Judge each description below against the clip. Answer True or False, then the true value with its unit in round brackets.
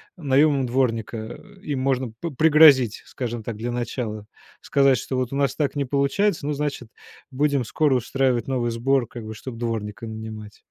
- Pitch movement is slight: False (3.4 semitones)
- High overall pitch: False (130 Hz)